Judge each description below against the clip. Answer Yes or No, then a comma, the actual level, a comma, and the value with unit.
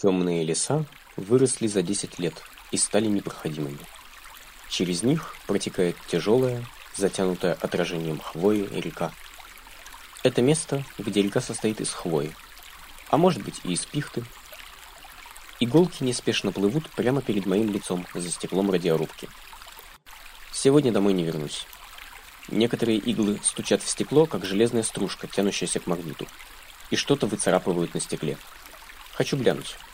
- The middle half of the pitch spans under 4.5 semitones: No, average, 5.0 semitones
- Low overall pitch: Yes, low, 100 Hz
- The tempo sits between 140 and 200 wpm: No, average, 125 wpm